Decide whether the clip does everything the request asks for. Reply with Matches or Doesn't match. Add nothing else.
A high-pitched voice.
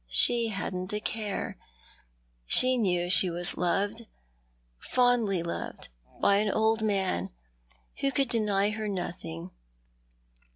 Matches